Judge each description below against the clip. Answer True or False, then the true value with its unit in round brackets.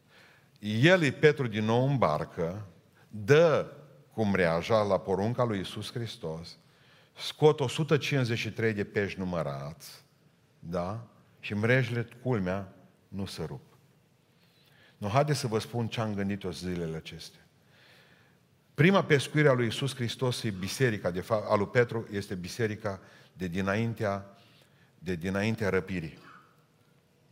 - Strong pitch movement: True (6.0 semitones)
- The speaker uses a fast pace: False (125 wpm)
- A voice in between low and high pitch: False (115 Hz)